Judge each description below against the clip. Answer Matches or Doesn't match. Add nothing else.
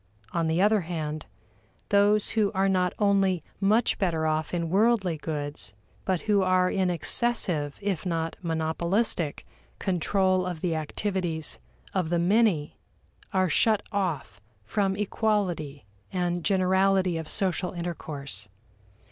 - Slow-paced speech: Matches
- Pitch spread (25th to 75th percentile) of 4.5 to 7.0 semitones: Doesn't match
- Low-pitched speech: Doesn't match